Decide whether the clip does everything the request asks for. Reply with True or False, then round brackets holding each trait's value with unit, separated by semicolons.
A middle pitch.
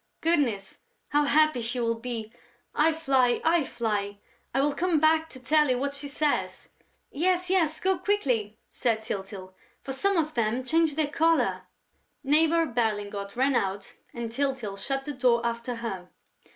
False (265 Hz)